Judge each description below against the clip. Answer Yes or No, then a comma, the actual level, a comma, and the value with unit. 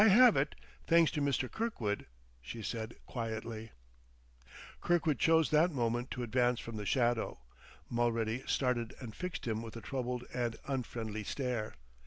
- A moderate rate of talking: Yes, average, 150 wpm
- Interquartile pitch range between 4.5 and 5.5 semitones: No, average, 3.9 semitones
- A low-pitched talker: Yes, low, 120 Hz